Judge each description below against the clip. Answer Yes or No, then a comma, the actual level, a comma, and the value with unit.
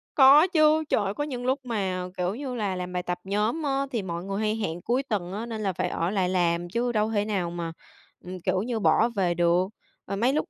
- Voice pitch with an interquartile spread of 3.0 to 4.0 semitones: No, average, 5.3 semitones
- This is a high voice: Yes, high, 205 Hz